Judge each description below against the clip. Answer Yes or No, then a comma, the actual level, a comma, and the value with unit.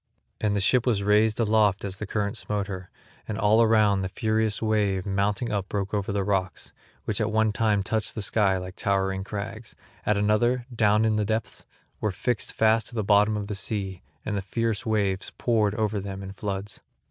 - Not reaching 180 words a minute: No, average, 200 wpm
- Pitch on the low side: Yes, low, 105 Hz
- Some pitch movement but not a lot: No, narrow, 1.8 semitones